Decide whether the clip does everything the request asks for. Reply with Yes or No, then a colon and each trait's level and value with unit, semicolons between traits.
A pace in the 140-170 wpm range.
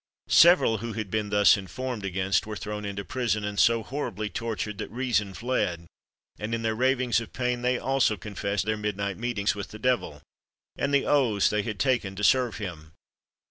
No: average, 185 wpm